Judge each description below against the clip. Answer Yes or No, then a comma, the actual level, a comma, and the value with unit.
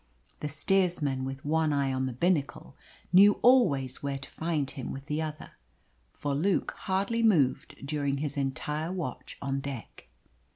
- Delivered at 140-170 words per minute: Yes, average, 155 wpm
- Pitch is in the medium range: Yes, medium, 145 Hz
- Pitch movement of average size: Yes, average, 4.0 semitones